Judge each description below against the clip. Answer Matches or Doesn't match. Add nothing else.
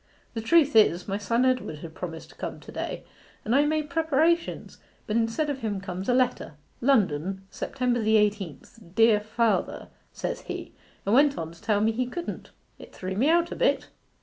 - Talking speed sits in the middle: Matches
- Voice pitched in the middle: Doesn't match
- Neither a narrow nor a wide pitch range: Doesn't match